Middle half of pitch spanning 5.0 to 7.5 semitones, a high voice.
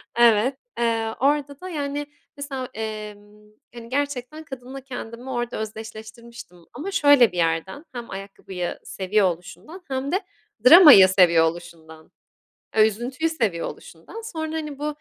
Yes: wide, 5.6 semitones; high, 235 Hz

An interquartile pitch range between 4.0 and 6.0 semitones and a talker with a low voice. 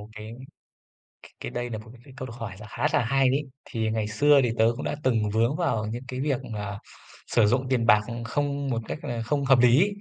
No: average, 3.4 semitones; low, 120 Hz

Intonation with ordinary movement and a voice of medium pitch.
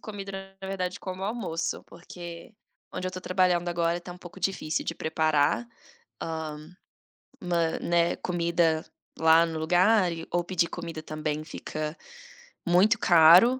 No: narrow, 2.2 semitones; medium, 175 Hz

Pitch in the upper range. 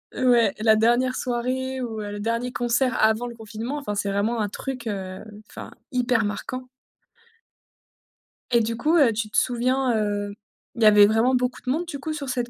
Yes: high, 235 Hz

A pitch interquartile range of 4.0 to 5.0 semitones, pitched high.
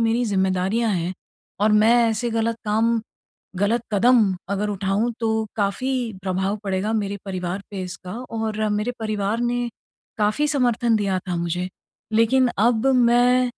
No: average, 3.1 semitones; high, 215 Hz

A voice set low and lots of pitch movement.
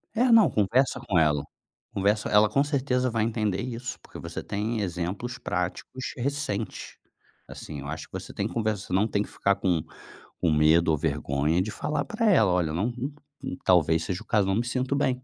Yes: low, 105 Hz; wide, 5.9 semitones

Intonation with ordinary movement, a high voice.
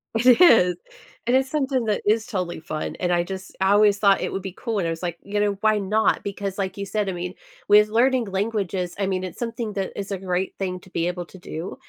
Yes: average, 3.0 semitones; high, 195 Hz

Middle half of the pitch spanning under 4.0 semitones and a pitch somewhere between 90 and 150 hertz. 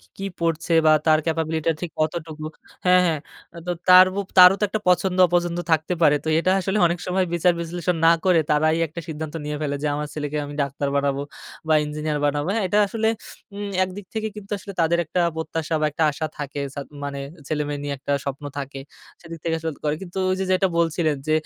No: average, 3.3 semitones; medium, 160 Hz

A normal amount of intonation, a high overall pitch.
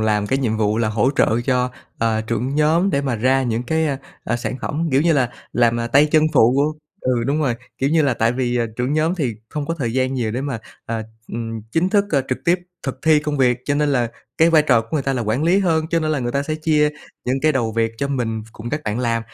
No: average, 4.5 semitones; low, 130 Hz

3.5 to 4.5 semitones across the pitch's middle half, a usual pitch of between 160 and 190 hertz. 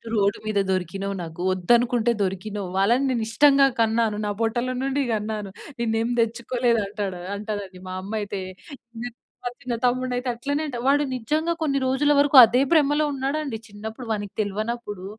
No: average, 4.0 semitones; high, 230 Hz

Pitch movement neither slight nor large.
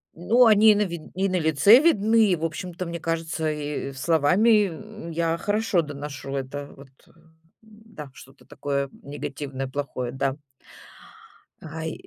No: wide, 6.2 semitones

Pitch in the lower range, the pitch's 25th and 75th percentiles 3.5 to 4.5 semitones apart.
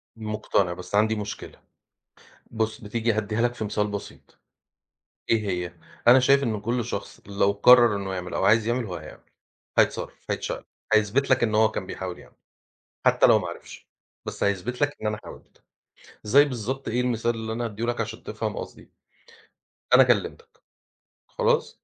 No: low, 110 Hz; average, 3.1 semitones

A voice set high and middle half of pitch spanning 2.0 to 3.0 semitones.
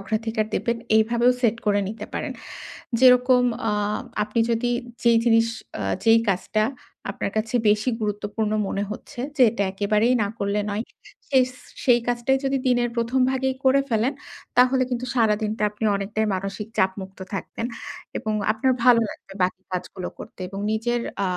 Yes: high, 225 Hz; average, 2.7 semitones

